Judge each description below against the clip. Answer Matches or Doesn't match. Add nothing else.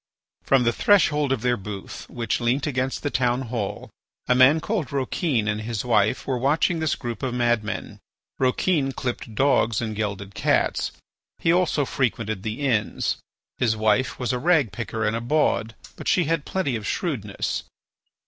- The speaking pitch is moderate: Doesn't match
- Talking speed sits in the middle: Matches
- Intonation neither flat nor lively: Matches